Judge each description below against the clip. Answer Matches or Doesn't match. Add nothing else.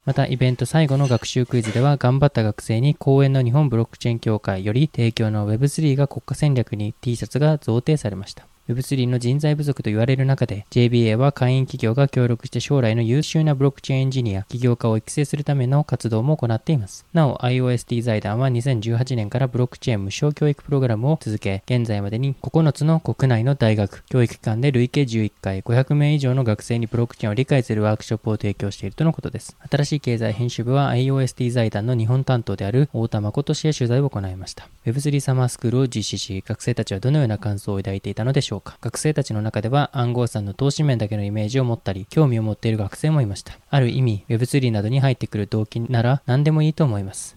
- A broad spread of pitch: Doesn't match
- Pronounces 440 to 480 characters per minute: Matches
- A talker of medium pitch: Doesn't match